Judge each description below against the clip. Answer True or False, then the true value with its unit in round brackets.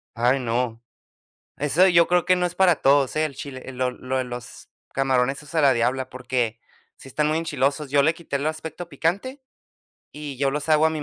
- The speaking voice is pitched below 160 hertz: True (140 Hz)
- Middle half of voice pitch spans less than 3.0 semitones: False (3.7 semitones)